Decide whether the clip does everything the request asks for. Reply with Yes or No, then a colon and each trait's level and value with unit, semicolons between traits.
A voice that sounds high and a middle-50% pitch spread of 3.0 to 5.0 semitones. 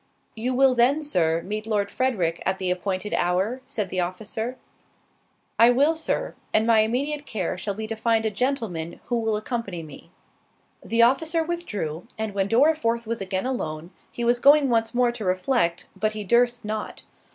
Yes: high, 220 Hz; average, 4.6 semitones